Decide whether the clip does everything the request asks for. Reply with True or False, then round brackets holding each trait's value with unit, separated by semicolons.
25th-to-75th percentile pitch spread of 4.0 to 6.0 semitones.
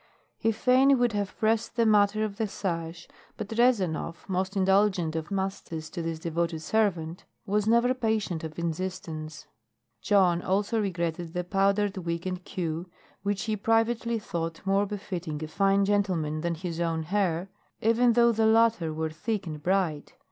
True (4.3 semitones)